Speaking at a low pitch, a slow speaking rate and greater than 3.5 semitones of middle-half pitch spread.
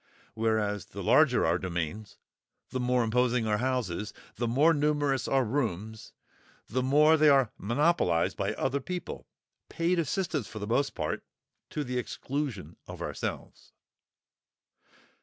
Yes: low, 125 Hz; slow, 125 wpm; average, 5.2 semitones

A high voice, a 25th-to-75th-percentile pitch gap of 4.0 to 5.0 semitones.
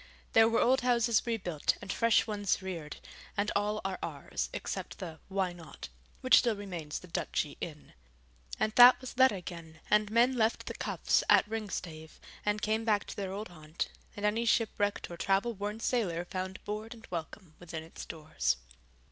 Yes: high, 205 Hz; average, 4.3 semitones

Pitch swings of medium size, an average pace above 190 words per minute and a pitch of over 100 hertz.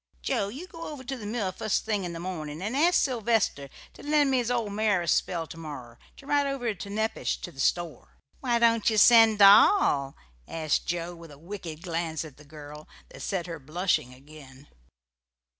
No: wide, 6.7 semitones; average, 200 wpm; medium, 185 Hz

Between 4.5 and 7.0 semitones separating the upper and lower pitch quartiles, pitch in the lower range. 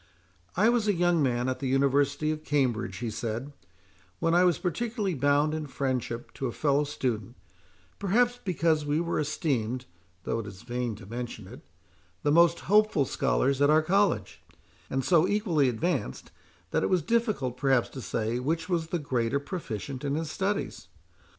No: wide, 5.5 semitones; medium, 145 Hz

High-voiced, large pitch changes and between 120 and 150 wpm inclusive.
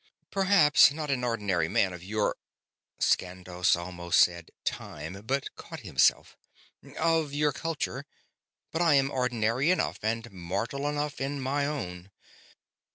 No: low, 125 Hz; wide, 8.0 semitones; average, 140 wpm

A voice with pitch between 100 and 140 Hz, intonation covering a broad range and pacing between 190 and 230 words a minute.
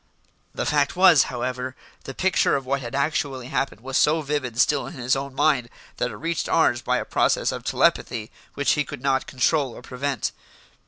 No: low, 135 Hz; narrow, 2.6 semitones; average, 195 wpm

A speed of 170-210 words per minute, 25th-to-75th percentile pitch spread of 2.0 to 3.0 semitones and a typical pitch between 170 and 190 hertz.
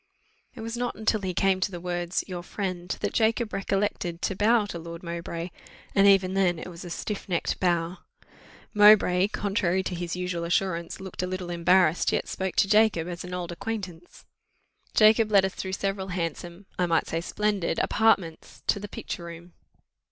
Yes: average, 185 wpm; narrow, 2.6 semitones; medium, 185 Hz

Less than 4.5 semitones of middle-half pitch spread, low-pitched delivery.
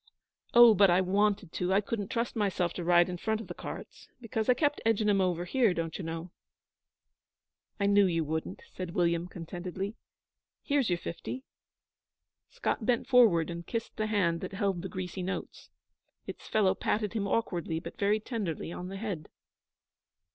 No: average, 3.8 semitones; high, 195 Hz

